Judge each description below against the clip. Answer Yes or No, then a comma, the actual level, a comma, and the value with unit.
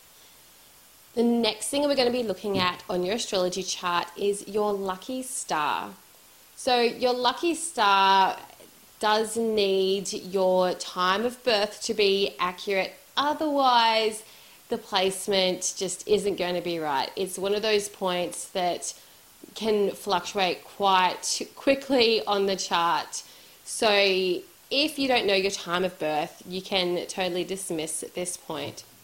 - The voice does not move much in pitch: No, average, 3.3 semitones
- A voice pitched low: No, high, 195 Hz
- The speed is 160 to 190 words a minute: No, average, 140 wpm